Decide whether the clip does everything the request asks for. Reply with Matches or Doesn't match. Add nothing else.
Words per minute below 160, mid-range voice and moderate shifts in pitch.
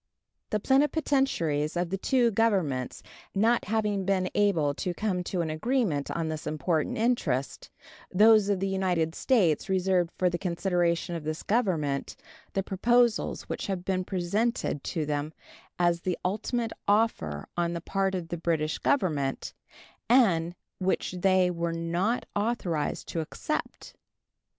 Matches